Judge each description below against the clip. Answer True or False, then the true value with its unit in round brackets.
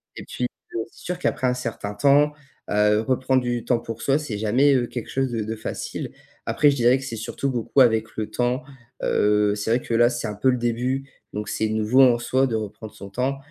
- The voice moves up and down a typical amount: True (3.1 semitones)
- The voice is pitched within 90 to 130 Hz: True (120 Hz)